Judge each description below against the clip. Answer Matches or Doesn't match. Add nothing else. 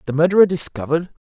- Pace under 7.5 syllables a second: Doesn't match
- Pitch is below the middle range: Doesn't match